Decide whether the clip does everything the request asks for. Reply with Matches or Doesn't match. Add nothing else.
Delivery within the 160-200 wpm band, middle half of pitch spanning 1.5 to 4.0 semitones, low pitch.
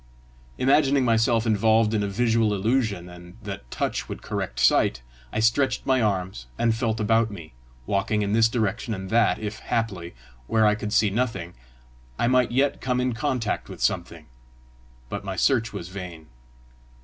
Matches